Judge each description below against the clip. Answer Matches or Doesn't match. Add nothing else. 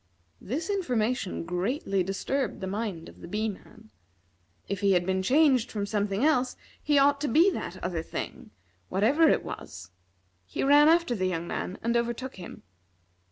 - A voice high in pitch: Matches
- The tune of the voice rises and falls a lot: Matches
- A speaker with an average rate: Matches